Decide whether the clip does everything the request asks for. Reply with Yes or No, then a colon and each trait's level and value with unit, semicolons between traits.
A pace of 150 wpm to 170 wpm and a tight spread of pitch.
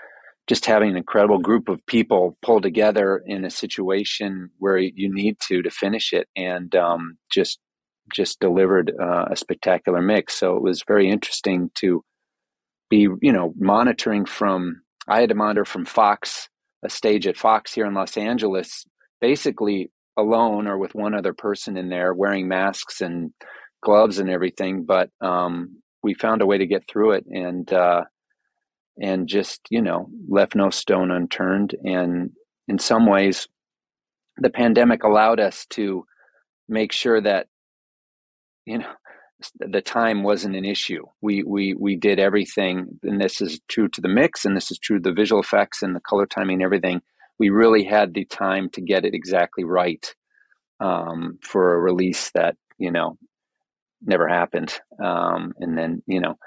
Yes: average, 165 wpm; narrow, 2.3 semitones